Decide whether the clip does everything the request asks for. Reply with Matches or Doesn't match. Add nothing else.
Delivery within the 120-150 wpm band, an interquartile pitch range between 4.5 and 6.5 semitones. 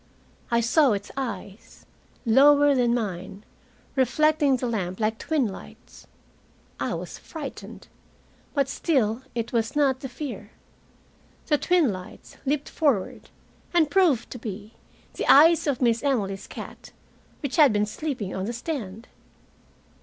Matches